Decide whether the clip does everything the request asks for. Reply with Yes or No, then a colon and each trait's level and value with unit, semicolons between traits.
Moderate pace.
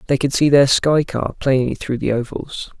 No: fast, 215 wpm